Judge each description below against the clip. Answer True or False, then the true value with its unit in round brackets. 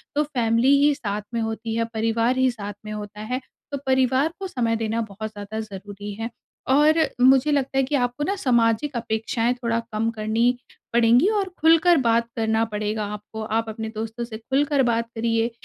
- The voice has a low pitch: False (230 Hz)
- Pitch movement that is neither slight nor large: True (3.1 semitones)